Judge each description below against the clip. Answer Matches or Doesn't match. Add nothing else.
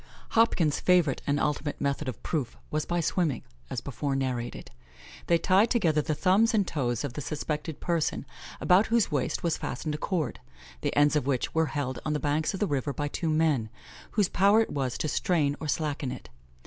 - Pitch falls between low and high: Matches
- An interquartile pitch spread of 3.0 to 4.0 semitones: Matches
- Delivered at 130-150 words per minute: Doesn't match